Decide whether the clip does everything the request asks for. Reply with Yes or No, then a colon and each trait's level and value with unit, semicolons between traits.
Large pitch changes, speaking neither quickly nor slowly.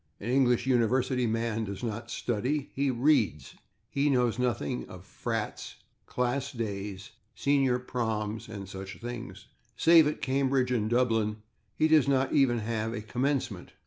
No: average, 3.4 semitones; average, 145 wpm